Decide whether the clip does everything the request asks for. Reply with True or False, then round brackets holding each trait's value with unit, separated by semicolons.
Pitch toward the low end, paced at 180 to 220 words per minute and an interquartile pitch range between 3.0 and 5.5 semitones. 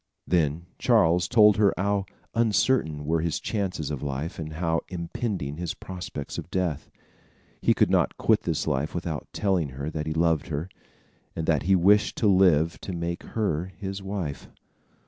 False (85 Hz; 165 wpm; 3.8 semitones)